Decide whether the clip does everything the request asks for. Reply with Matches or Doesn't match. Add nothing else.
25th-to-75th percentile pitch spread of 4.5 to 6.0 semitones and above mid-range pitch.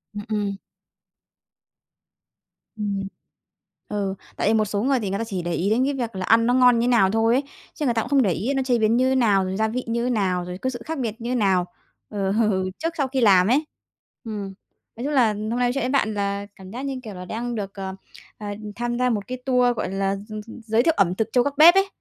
Doesn't match